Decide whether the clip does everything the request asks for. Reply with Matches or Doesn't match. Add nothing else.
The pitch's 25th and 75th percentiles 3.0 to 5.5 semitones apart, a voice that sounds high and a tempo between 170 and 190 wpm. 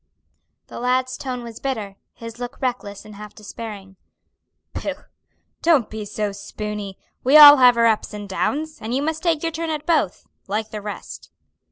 Matches